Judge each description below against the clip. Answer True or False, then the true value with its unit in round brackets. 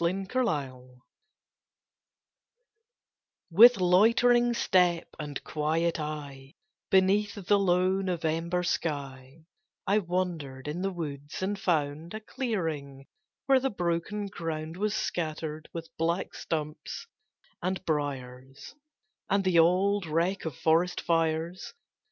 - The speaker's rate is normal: False (110 wpm)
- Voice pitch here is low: False (170 Hz)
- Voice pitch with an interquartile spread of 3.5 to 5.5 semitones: True (4.0 semitones)